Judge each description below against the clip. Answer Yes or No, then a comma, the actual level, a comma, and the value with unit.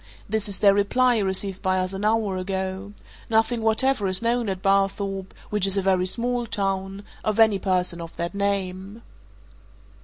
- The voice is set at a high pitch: Yes, high, 195 Hz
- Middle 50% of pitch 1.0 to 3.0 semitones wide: Yes, narrow, 2.5 semitones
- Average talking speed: Yes, average, 165 wpm